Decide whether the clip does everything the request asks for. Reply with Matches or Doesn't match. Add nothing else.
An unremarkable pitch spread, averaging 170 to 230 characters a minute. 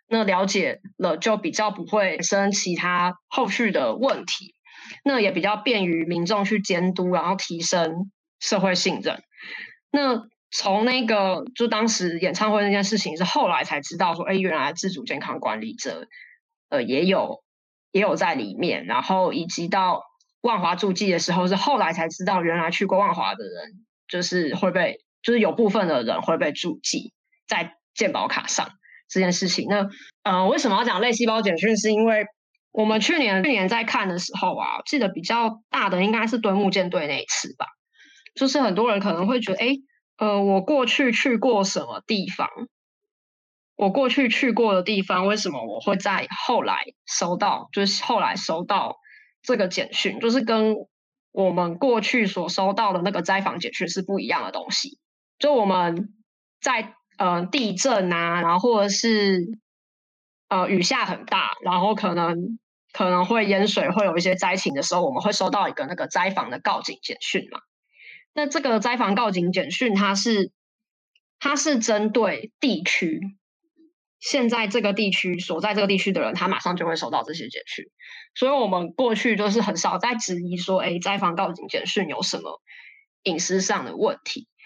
Doesn't match